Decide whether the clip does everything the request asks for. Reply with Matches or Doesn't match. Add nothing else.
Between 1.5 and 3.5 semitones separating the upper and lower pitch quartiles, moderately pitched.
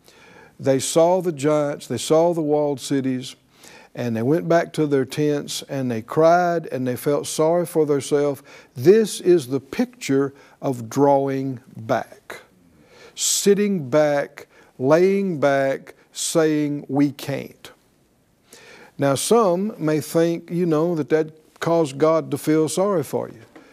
Matches